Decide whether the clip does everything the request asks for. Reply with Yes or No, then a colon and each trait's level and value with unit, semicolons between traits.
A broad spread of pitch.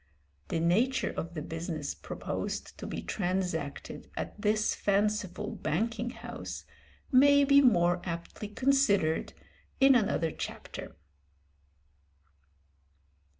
Yes: wide, 6.0 semitones